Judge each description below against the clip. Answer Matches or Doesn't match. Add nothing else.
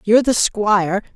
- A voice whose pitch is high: Matches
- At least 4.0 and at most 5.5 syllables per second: Matches